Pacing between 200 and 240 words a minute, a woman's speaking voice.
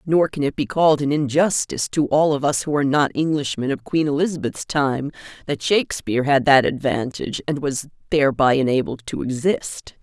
No: average, 180 wpm; female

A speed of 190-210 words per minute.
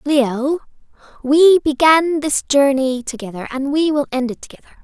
No: average, 150 wpm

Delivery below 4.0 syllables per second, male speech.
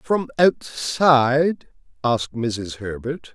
Yes: 3.2 syllables/s; male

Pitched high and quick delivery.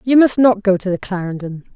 Yes: high, 205 Hz; fast, 240 wpm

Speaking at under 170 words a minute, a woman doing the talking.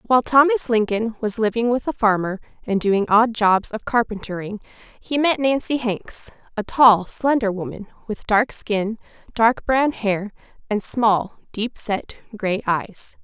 Yes: average, 155 wpm; female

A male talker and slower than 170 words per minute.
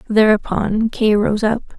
No: female; slow, 135 wpm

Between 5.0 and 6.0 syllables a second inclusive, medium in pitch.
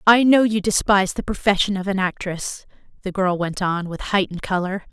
No: 5.5 syllables/s; high, 195 Hz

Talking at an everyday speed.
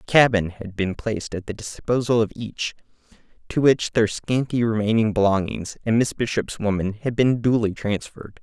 Yes: average, 170 wpm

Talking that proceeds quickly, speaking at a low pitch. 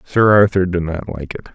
Yes: fast, 235 wpm; very low, 90 Hz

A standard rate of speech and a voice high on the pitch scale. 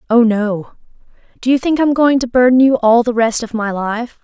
No: fast, 225 wpm; high, 240 Hz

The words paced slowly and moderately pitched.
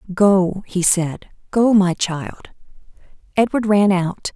No: slow, 125 wpm; high, 195 Hz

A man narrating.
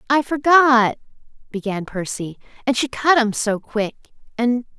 No: female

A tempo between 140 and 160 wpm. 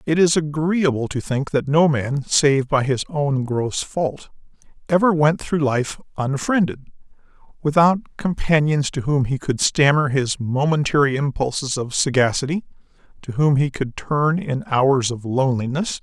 Yes: average, 150 wpm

